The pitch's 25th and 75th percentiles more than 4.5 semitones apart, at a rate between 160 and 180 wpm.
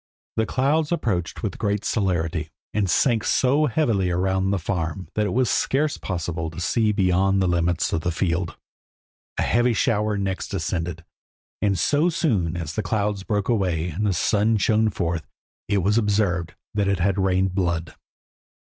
No: average, 3.7 semitones; average, 165 wpm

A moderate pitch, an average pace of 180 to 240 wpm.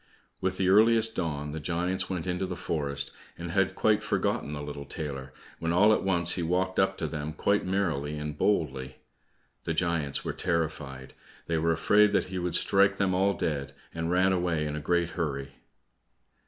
No: very low, 85 Hz; average, 185 wpm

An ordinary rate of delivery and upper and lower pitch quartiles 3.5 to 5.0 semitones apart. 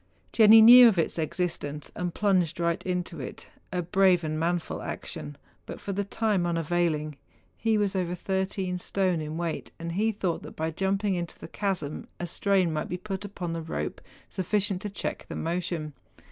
No: average, 190 wpm; average, 2.9 semitones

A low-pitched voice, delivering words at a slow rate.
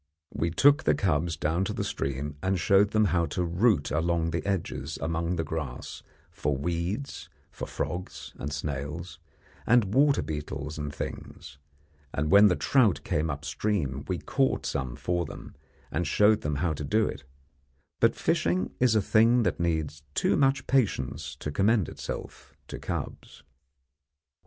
No: very low, 85 Hz; average, 155 wpm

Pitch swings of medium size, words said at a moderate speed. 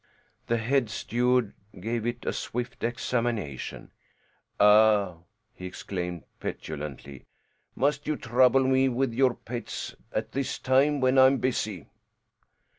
No: average, 3.9 semitones; slow, 120 wpm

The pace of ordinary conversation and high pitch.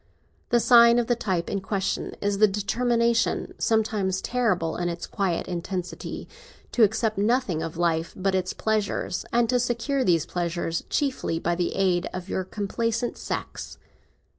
Yes: average, 145 wpm; high, 200 Hz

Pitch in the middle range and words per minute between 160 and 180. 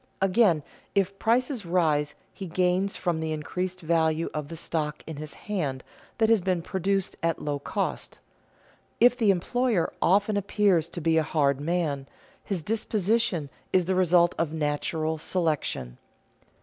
No: medium, 175 Hz; average, 150 wpm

